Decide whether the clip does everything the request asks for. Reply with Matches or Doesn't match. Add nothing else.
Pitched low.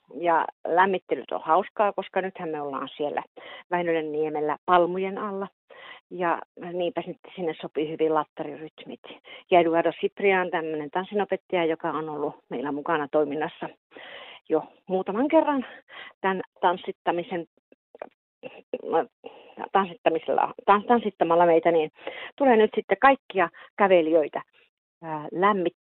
Doesn't match